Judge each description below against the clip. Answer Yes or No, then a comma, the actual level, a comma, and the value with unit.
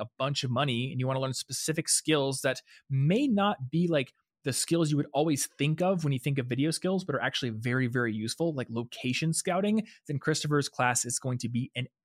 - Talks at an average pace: No, fast, 230 wpm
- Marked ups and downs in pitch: No, average, 4.0 semitones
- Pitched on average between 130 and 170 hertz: Yes, low, 135 Hz